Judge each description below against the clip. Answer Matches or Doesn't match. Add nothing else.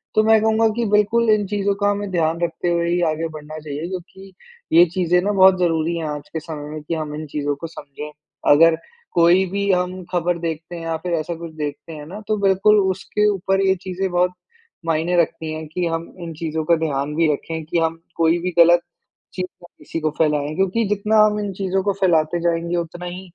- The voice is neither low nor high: Matches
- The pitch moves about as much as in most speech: Matches